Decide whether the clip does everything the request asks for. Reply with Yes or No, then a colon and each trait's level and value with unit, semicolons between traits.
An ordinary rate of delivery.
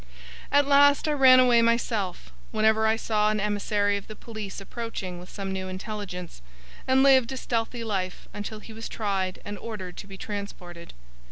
Yes: average, 175 wpm